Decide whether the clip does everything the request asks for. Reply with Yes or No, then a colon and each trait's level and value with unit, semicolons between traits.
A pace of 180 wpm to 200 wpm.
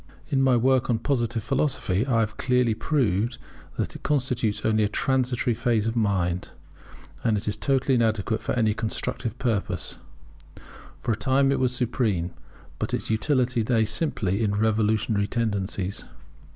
No: average, 150 wpm